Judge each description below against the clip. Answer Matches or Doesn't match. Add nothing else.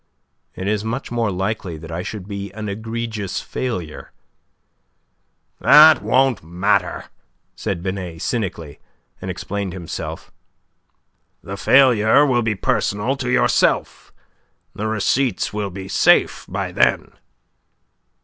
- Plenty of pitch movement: Doesn't match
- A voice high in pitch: Doesn't match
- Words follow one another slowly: Matches